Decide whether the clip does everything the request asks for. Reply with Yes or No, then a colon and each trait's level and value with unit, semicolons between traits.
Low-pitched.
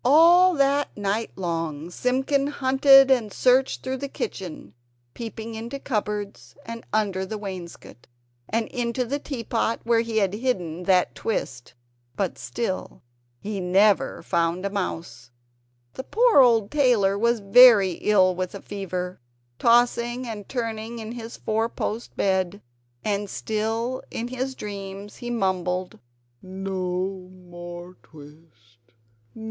No: high, 210 Hz